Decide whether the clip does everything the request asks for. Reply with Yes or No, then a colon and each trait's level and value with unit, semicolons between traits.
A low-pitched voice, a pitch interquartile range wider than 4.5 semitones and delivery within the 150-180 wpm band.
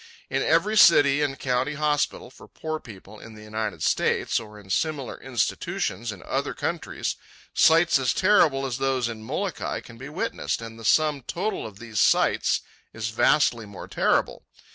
Yes: low, 125 Hz; average, 5.2 semitones; average, 165 wpm